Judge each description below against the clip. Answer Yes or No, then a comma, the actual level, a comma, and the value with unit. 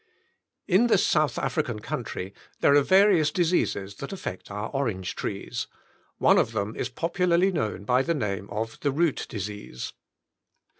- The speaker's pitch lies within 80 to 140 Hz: Yes, low, 135 Hz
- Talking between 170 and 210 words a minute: No, average, 150 wpm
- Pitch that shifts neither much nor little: No, wide, 8.5 semitones